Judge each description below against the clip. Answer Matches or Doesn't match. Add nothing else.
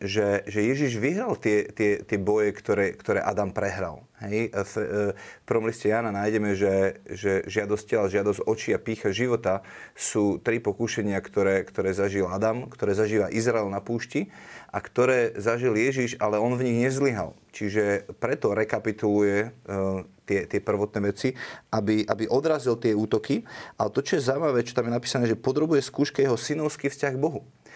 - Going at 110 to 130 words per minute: Doesn't match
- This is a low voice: Matches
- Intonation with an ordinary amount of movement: Matches